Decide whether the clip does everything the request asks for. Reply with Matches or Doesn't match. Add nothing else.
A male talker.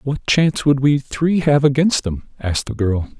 Matches